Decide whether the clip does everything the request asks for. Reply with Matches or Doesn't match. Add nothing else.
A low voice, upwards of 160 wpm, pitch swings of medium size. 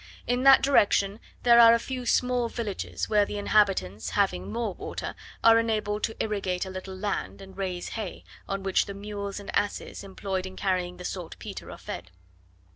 Doesn't match